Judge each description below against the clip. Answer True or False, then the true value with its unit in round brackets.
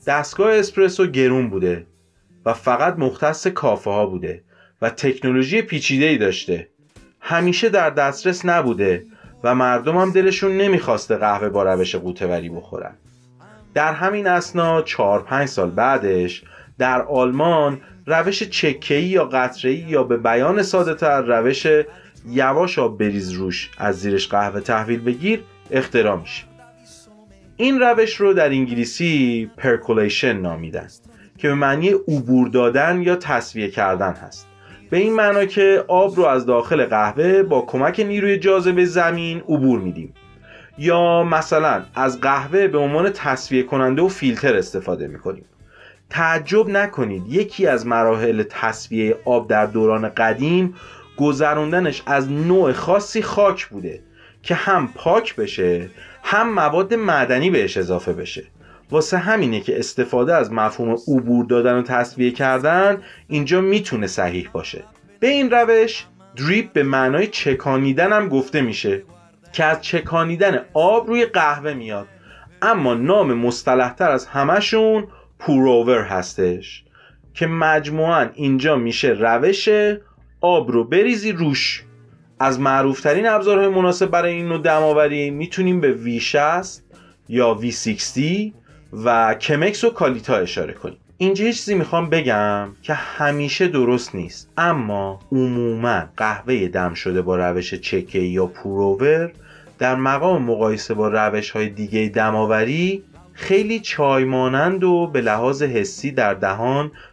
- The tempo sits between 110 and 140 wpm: True (130 wpm)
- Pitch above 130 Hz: True (140 Hz)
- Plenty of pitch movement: True (7.9 semitones)